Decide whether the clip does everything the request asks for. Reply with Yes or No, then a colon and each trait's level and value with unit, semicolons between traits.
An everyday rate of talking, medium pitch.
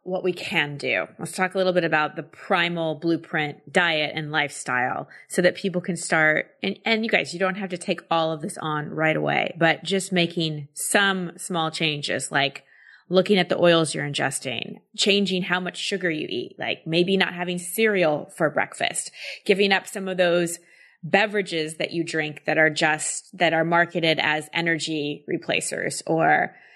Yes: average, 180 wpm; medium, 170 Hz